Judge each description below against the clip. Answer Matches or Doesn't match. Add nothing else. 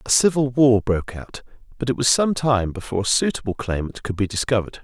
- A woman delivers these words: Doesn't match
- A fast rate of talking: Matches